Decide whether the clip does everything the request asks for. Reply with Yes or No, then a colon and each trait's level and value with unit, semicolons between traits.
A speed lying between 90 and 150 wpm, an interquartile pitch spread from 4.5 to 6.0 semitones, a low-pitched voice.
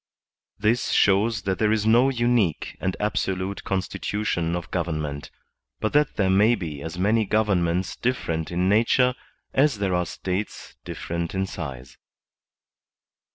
No: average, 140 wpm; average, 4.0 semitones; very low, 95 Hz